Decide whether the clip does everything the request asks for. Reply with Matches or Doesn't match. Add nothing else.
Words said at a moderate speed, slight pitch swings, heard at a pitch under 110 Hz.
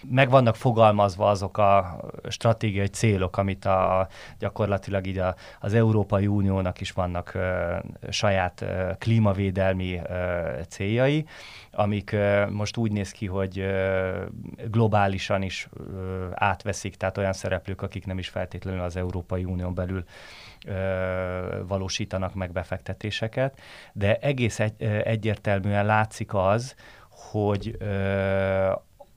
Matches